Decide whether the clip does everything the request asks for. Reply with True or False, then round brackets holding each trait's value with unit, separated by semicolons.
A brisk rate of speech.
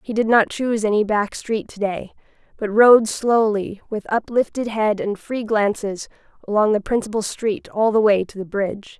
False (185 wpm)